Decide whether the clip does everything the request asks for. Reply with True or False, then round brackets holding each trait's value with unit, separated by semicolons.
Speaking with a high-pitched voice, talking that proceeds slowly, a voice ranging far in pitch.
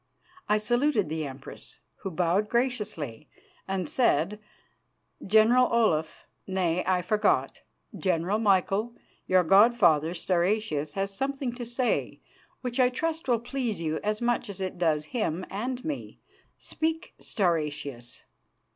True (200 Hz; 130 wpm; 6.2 semitones)